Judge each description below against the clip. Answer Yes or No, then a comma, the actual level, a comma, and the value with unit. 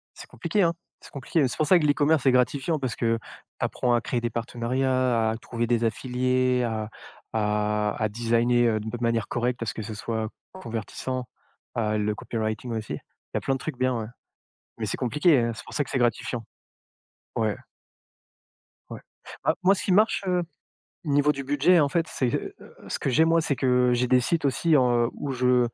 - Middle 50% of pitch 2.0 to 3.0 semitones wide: No, average, 3.5 semitones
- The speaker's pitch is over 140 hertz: No, low, 125 Hz